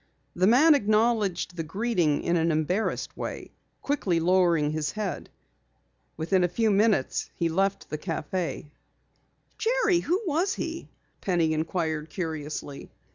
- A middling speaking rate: No, slow, 130 wpm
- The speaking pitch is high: No, medium, 180 Hz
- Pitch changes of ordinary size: No, wide, 5.7 semitones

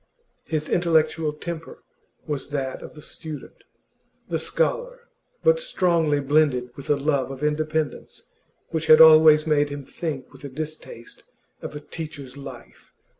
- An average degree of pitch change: No, narrow, 2.2 semitones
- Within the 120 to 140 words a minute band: Yes, slow, 135 wpm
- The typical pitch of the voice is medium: Yes, medium, 155 Hz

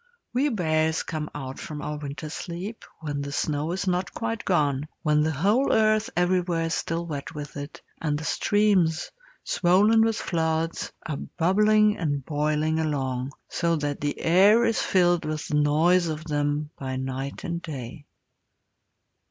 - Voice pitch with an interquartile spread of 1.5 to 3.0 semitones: No, average, 3.7 semitones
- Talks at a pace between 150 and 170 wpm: Yes, average, 160 wpm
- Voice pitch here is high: No, medium, 160 Hz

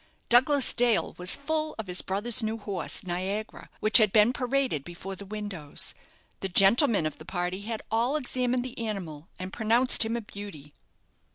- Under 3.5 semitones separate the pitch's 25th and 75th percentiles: No, average, 4.6 semitones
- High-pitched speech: Yes, high, 215 Hz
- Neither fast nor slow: Yes, average, 170 wpm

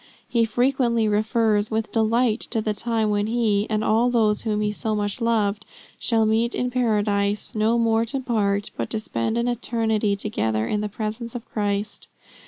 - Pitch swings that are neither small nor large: No, narrow, 1.9 semitones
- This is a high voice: Yes, high, 220 Hz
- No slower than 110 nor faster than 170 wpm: No, average, 180 wpm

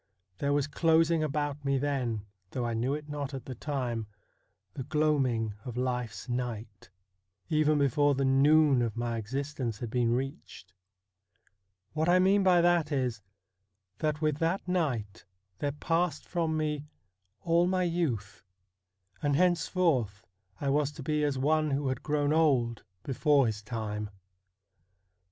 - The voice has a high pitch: No, medium, 140 Hz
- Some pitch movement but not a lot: Yes, average, 4.1 semitones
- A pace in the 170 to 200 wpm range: No, average, 145 wpm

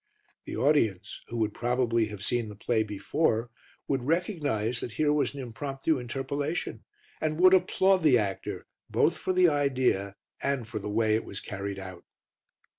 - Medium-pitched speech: No, low, 125 Hz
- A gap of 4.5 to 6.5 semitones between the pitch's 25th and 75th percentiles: Yes, average, 5.3 semitones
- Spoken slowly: No, average, 165 wpm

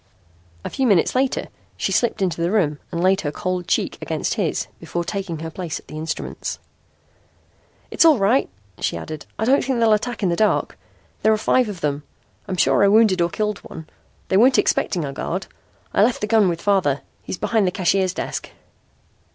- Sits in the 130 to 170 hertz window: No, high, 190 Hz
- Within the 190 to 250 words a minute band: Yes, average, 200 wpm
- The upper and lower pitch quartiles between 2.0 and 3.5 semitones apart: No, average, 4.3 semitones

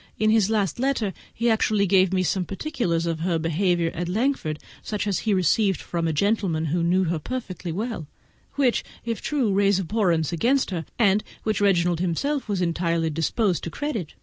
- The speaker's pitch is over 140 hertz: Yes, high, 190 Hz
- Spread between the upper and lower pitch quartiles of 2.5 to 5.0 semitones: Yes, average, 4.5 semitones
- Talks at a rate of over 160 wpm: Yes, average, 185 wpm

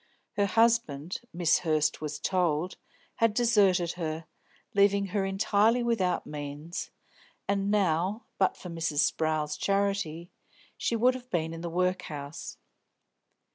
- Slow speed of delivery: Yes, slow, 125 wpm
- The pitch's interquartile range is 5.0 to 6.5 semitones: No, average, 4.1 semitones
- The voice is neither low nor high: Yes, medium, 180 Hz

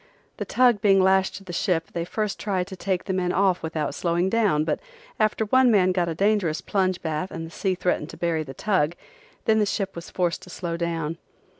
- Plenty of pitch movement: No, average, 2.9 semitones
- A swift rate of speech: Yes, fast, 225 wpm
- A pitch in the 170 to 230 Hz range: Yes, medium, 185 Hz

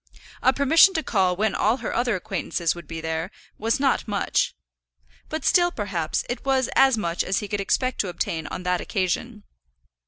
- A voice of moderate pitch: No, high, 210 Hz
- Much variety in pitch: Yes, wide, 6.3 semitones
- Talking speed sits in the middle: Yes, average, 185 wpm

